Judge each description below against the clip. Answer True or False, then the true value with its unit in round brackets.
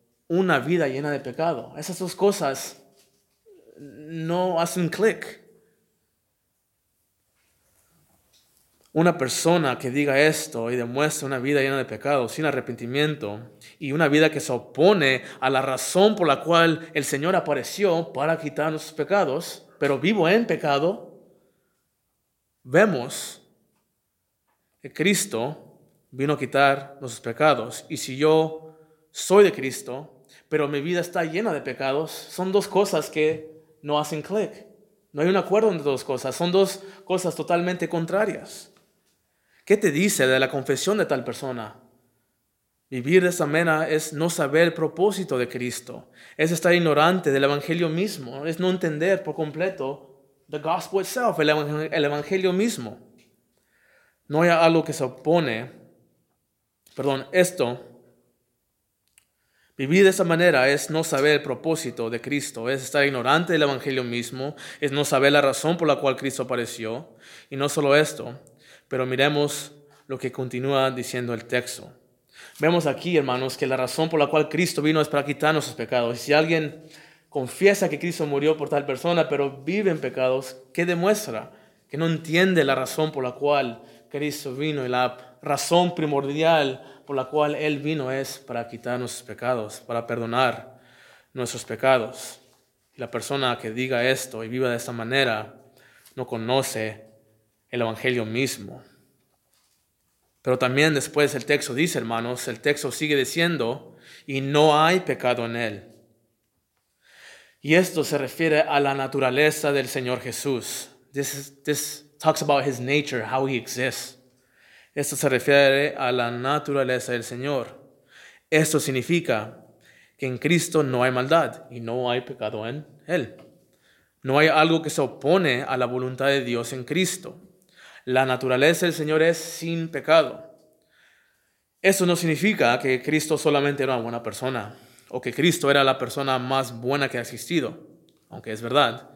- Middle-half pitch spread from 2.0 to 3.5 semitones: False (4.0 semitones)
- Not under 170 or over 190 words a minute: False (150 wpm)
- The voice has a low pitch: False (145 Hz)